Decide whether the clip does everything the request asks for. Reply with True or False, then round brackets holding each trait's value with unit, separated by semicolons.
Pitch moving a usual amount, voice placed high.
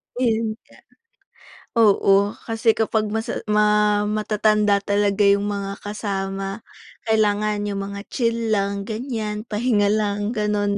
False (1.3 semitones; 210 Hz)